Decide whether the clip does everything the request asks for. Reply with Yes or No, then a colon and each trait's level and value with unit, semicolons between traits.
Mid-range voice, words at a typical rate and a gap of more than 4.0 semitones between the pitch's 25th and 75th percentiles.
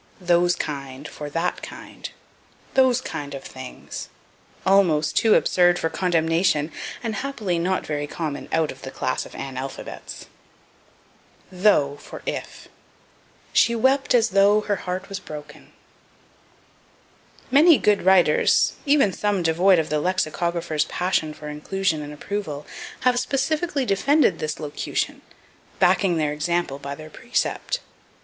No: medium, 175 Hz; slow, 130 wpm; average, 5.3 semitones